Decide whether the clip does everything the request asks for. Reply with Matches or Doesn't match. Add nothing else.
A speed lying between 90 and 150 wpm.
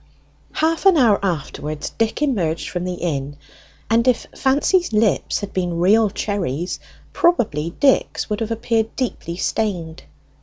Matches